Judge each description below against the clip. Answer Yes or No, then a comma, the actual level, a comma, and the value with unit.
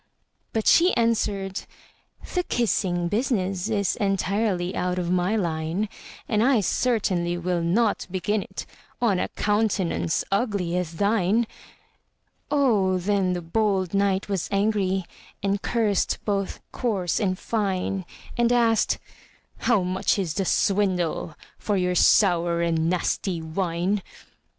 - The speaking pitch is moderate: No, high, 195 Hz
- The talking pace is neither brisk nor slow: No, slow, 125 wpm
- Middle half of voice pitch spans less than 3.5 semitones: Yes, average, 3.0 semitones